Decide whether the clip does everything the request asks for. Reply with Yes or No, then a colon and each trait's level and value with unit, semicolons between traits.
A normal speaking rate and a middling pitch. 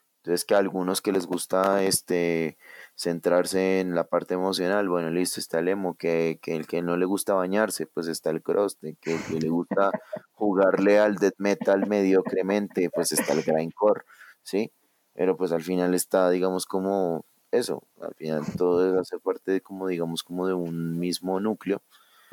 No: average, 180 wpm; very low, 95 Hz